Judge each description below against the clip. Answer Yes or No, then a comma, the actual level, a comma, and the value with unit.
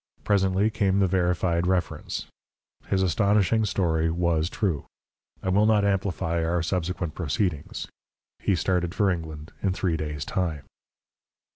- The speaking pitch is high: No, very low, 90 Hz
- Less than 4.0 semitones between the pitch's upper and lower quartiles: Yes, average, 2.9 semitones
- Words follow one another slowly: Yes, slow, 130 wpm